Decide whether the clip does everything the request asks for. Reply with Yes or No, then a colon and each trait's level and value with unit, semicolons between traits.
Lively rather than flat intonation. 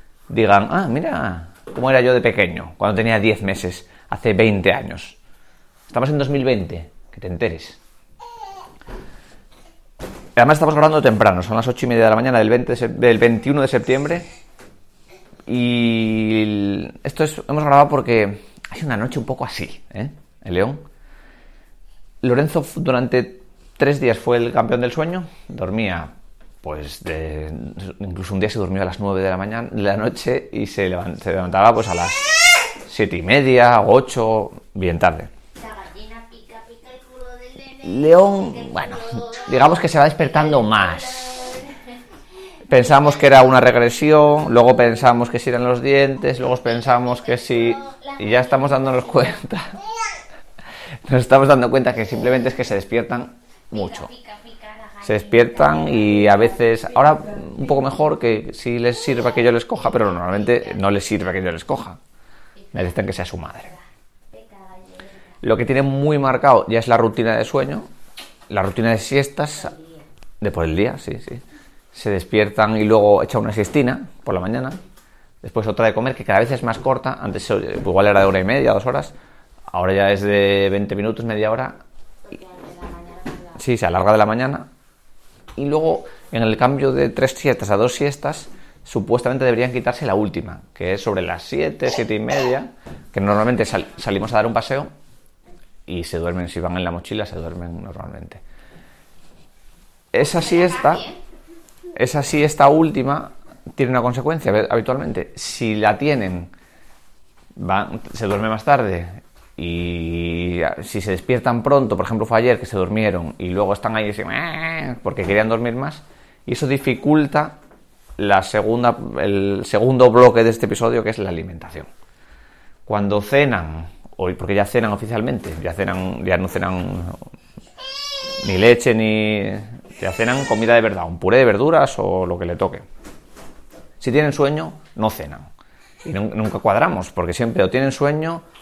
Yes: wide, 5.7 semitones